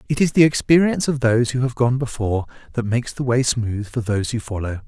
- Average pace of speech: No, fast, 235 wpm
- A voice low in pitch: Yes, low, 120 Hz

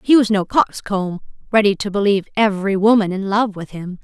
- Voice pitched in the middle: No, high, 200 Hz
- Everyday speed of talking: Yes, average, 195 wpm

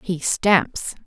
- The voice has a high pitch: No, medium, 180 Hz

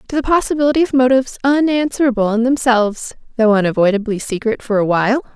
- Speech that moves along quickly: No, average, 155 wpm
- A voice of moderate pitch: No, high, 240 Hz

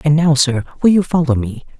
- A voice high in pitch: No, medium, 150 Hz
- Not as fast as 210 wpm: No, fast, 235 wpm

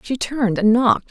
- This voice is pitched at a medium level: No, high, 235 Hz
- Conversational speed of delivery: No, fast, 220 wpm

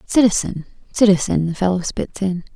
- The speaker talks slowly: Yes, slow, 115 wpm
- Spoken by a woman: Yes, female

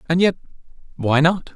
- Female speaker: No, male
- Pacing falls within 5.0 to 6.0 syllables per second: Yes, 5.6 syllables/s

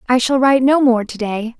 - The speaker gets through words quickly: Yes, fast, 265 wpm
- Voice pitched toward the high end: Yes, high, 245 Hz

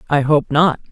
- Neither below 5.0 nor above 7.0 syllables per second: Yes, 5.1 syllables/s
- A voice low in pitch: No, medium, 150 Hz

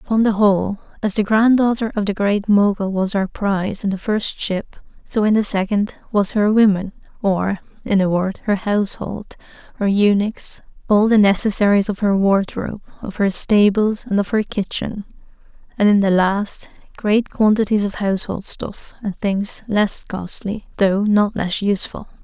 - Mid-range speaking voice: No, high, 205 Hz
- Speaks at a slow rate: No, average, 165 wpm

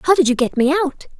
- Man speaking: No, female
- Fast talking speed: Yes, fast, 300 wpm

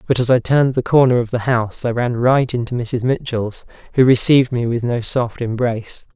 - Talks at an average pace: No, fast, 215 wpm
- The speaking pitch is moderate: No, low, 120 Hz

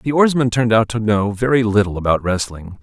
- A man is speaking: Yes, male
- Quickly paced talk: Yes, fast, 210 wpm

